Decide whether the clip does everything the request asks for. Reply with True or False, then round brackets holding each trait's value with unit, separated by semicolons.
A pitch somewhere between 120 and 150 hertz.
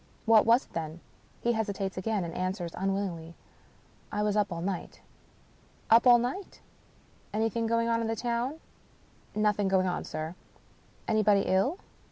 False (210 Hz)